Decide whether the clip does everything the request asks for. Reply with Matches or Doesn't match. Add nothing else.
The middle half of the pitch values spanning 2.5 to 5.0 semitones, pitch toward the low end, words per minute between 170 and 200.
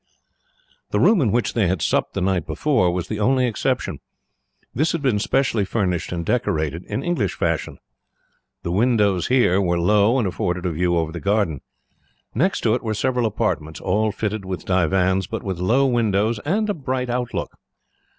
Doesn't match